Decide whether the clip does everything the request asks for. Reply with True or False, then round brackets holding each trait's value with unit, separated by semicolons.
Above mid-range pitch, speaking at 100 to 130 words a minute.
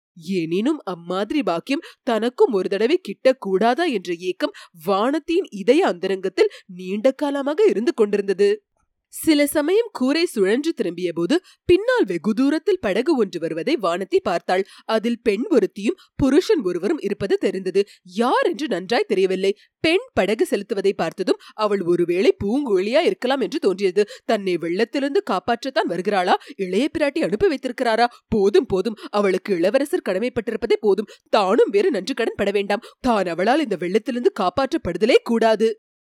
True (235 Hz; 125 wpm)